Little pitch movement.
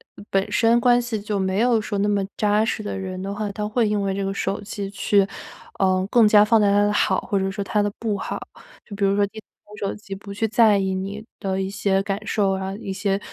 Yes: narrow, 1.4 semitones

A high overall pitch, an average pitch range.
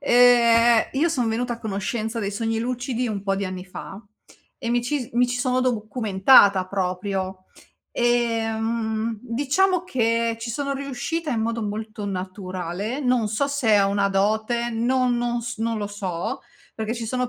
Yes: high, 230 Hz; average, 3.2 semitones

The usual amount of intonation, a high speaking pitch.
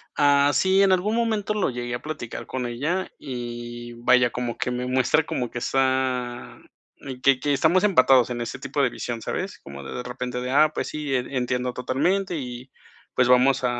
No: average, 3.2 semitones; low, 130 Hz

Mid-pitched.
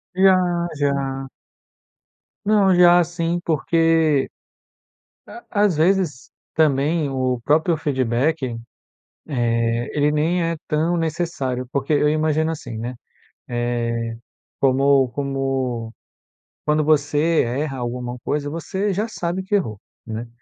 Yes: medium, 150 Hz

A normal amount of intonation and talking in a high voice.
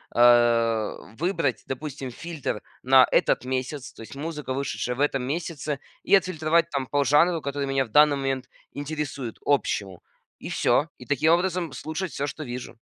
No: average, 3.4 semitones; medium, 140 Hz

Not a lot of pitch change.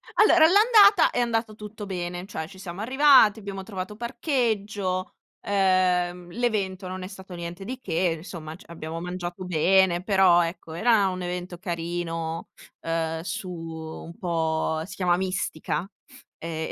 No: average, 3.3 semitones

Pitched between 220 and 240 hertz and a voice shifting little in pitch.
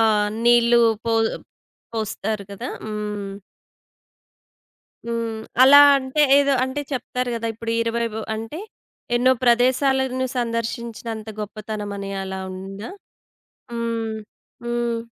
Yes: high, 230 Hz; narrow, 2.2 semitones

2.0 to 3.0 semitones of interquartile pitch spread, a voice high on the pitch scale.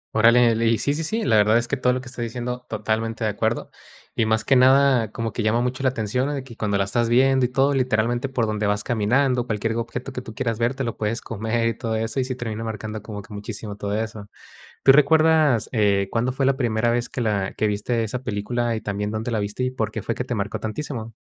No: narrow, 2.6 semitones; low, 115 Hz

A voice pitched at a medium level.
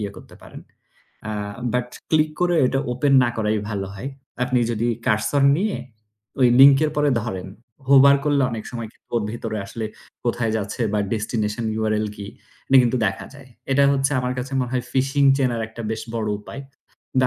No: low, 125 Hz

